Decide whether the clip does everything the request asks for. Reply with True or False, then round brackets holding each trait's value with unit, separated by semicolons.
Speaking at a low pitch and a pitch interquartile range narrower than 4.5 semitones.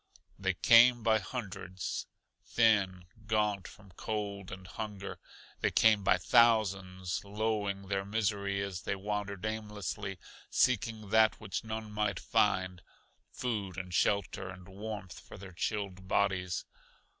True (100 Hz; 2.4 semitones)